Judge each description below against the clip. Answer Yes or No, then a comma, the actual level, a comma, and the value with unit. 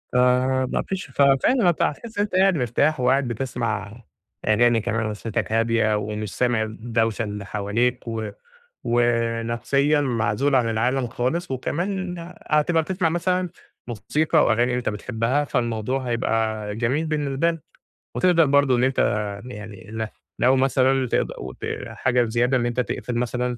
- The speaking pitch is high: No, low, 125 Hz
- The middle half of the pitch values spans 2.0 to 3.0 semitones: No, average, 3.8 semitones